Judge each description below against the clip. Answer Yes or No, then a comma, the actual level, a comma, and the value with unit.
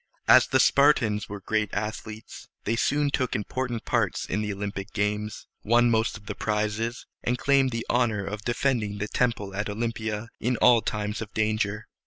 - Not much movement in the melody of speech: Yes, narrow, 2.3 semitones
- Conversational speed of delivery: Yes, average, 175 wpm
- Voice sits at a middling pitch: No, low, 110 Hz